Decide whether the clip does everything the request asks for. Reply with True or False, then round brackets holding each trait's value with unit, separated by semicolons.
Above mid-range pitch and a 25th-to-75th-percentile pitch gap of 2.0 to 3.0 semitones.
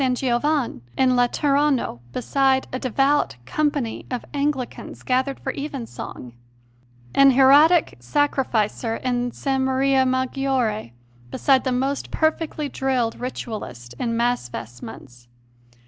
True (260 Hz; 2.7 semitones)